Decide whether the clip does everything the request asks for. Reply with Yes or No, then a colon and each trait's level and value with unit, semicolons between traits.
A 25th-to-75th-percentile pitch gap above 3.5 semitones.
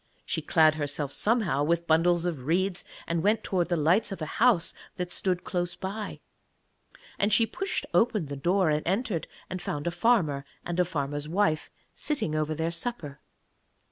Yes: average, 4.5 semitones